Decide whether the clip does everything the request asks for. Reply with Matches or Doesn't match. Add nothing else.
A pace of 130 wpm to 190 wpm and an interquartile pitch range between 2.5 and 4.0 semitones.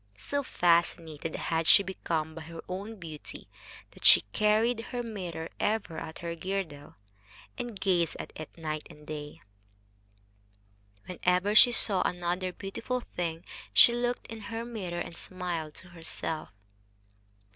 Doesn't match